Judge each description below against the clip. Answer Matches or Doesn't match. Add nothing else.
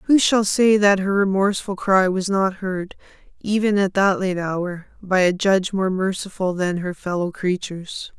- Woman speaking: Matches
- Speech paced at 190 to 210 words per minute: Doesn't match